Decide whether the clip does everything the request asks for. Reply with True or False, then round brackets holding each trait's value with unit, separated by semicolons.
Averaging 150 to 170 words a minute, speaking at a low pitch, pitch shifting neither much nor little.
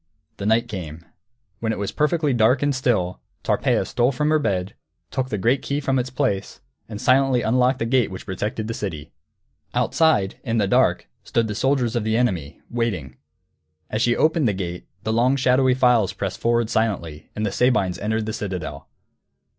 False (185 wpm; 115 Hz; 4.4 semitones)